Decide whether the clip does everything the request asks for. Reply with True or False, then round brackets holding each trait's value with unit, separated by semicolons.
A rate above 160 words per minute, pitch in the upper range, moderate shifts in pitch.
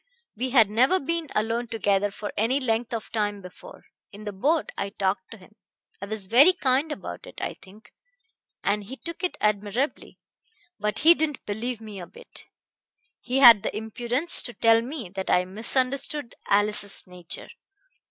True (170 wpm; 225 Hz; 4.5 semitones)